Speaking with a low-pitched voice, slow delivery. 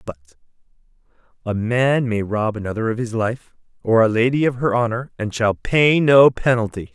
No: low, 115 Hz; average, 175 wpm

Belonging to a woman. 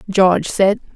Yes: female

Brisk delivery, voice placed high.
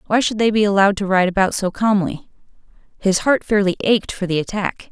Yes: fast, 210 wpm; high, 200 Hz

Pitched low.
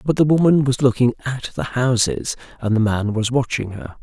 Yes: low, 120 Hz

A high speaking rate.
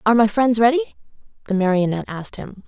No: average, 180 wpm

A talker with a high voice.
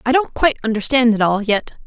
Yes: high, 235 Hz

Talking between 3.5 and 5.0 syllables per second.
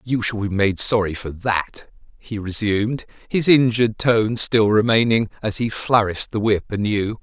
Yes: 4.6 syllables/s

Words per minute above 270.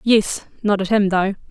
No: average, 200 wpm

